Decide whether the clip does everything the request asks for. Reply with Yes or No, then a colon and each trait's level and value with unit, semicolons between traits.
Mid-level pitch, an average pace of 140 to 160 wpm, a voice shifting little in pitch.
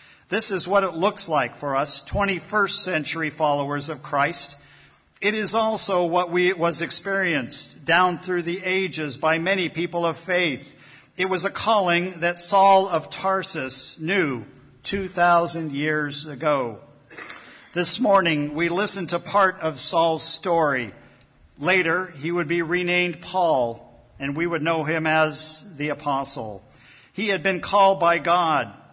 No: medium, 170 Hz; average, 145 wpm; average, 3.5 semitones